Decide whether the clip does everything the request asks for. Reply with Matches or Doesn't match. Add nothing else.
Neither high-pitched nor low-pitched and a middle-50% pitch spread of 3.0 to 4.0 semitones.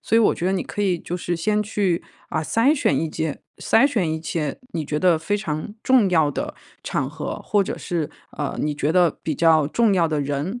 Doesn't match